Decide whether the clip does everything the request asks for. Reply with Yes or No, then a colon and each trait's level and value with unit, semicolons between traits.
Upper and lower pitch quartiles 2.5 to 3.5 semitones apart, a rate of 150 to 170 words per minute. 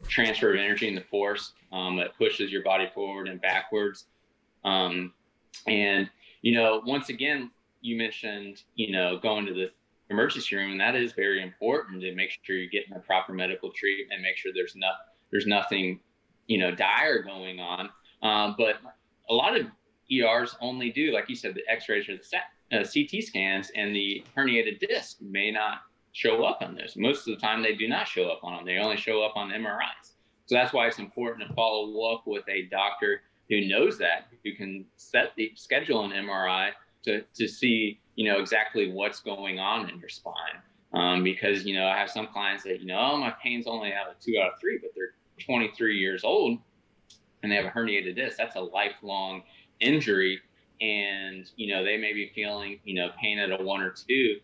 No: average, 3.0 semitones; fast, 205 wpm